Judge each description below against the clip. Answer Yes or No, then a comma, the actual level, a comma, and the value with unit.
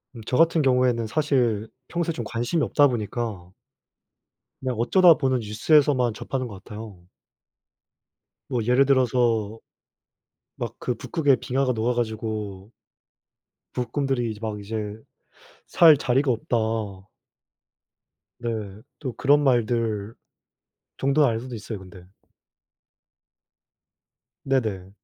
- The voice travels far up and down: No, average, 3.7 semitones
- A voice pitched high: No, low, 120 Hz